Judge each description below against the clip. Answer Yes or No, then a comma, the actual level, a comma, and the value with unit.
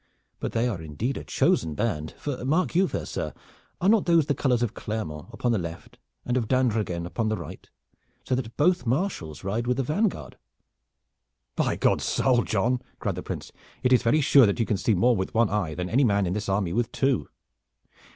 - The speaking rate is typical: No, fast, 210 wpm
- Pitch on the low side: Yes, low, 115 Hz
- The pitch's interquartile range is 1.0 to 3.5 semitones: No, average, 5.0 semitones